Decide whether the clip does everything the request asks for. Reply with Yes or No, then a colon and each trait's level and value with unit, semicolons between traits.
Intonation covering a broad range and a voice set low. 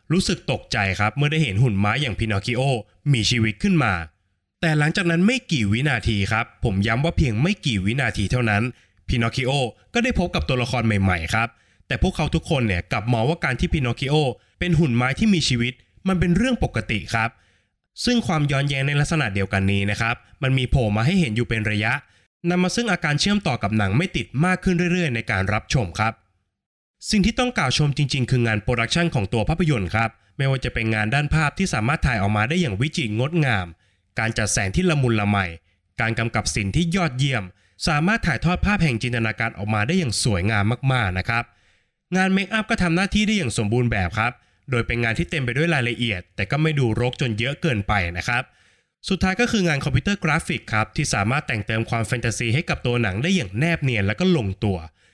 Yes: wide, 7.1 semitones; low, 125 Hz